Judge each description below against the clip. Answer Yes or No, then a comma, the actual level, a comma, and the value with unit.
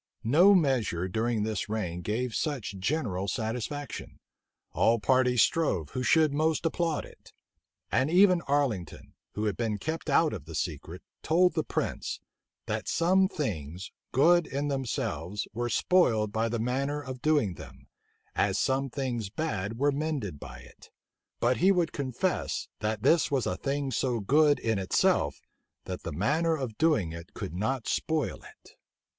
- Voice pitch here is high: No, low, 125 Hz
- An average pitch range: No, wide, 6.4 semitones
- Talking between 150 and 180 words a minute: Yes, average, 155 wpm